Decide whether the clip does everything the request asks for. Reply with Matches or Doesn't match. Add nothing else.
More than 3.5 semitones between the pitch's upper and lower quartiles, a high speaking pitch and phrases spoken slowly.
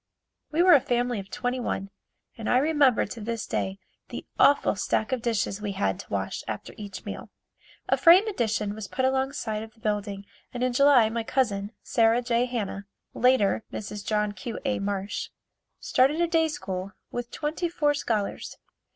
Doesn't match